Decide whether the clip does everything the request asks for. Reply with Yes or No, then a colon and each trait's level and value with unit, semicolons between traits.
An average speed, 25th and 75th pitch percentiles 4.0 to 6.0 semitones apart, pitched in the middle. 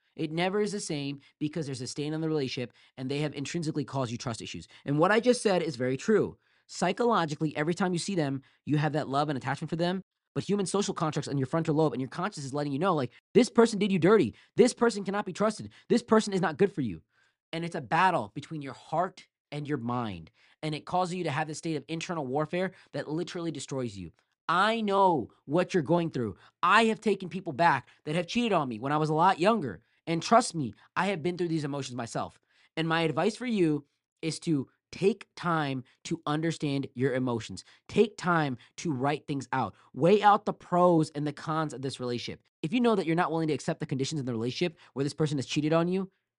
No: fast, 235 wpm; average, 4.6 semitones; medium, 160 Hz